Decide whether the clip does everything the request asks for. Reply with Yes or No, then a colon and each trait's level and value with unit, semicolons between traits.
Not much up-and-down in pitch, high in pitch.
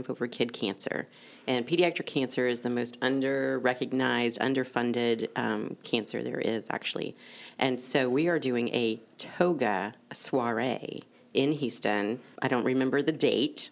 No: narrow, 1.9 semitones; low, 125 Hz